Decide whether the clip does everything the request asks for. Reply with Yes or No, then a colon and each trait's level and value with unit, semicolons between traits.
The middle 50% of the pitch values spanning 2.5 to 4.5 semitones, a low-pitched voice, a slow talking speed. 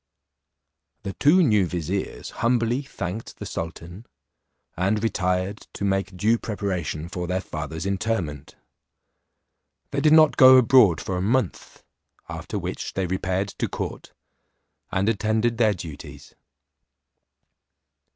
Yes: average, 4.1 semitones; low, 100 Hz; slow, 120 wpm